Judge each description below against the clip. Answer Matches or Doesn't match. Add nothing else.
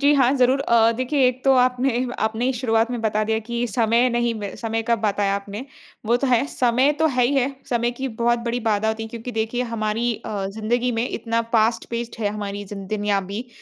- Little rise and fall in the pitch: Matches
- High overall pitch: Matches